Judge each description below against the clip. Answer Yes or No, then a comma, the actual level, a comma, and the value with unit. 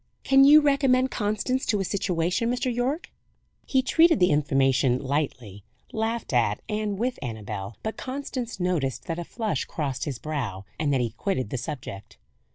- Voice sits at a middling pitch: Yes, medium, 180 Hz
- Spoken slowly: No, average, 165 wpm